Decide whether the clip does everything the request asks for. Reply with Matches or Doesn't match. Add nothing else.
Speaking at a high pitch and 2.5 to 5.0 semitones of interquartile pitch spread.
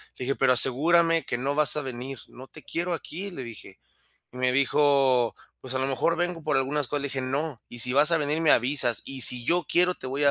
Doesn't match